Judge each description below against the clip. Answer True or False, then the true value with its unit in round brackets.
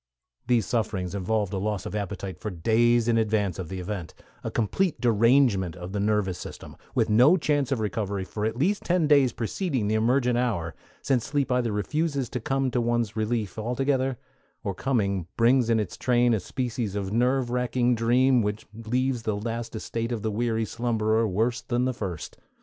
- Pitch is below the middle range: True (115 Hz)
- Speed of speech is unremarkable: True (185 wpm)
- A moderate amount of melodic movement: True (3.2 semitones)